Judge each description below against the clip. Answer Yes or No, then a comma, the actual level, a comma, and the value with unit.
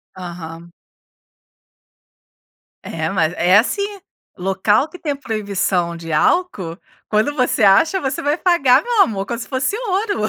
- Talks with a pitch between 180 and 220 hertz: Yes, high, 215 Hz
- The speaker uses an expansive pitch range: Yes, wide, 8.5 semitones